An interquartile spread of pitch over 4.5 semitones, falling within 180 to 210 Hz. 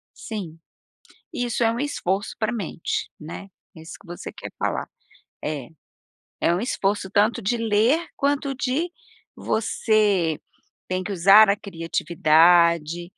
Yes: average, 5.2 semitones; high, 200 Hz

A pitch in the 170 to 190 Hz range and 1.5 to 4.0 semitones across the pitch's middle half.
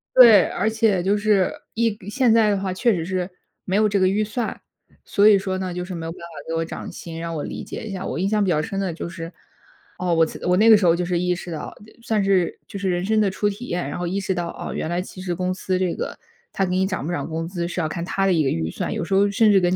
Yes: medium, 185 Hz; average, 2.8 semitones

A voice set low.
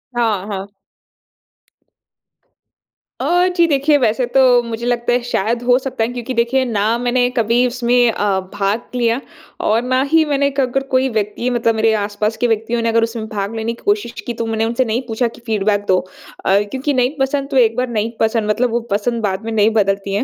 No: high, 230 Hz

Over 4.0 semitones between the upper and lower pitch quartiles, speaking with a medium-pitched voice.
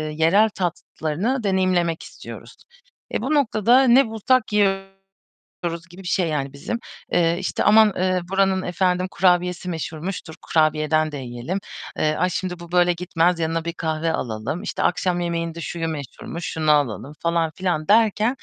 No: average, 3.2 semitones; medium, 175 Hz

